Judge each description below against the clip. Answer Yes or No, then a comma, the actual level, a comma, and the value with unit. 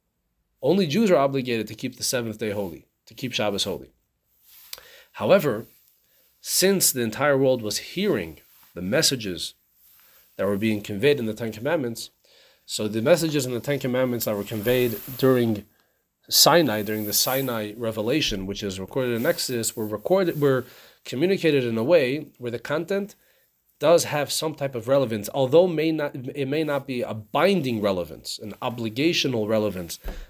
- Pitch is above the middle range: No, low, 125 Hz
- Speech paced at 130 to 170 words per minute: Yes, average, 160 wpm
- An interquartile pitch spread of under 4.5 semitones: No, average, 5.3 semitones